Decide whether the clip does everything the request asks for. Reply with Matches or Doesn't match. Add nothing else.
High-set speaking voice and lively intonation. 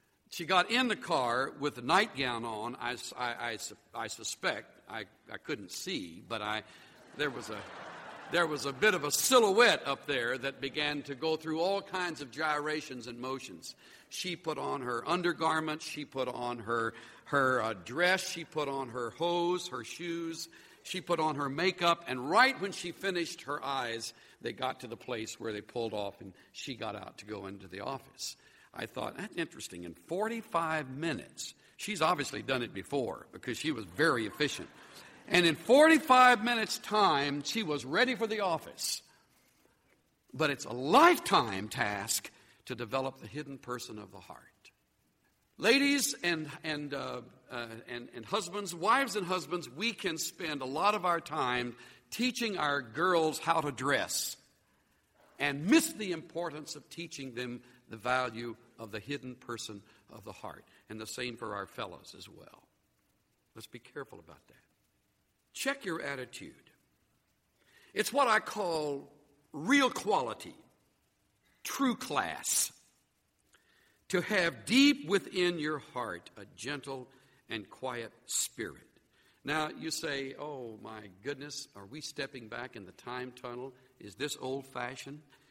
Doesn't match